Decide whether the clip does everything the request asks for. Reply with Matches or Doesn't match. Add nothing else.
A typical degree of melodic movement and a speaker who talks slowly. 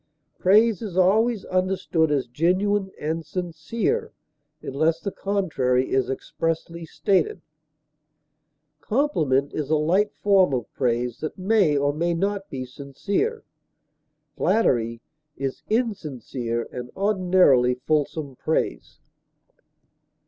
Doesn't match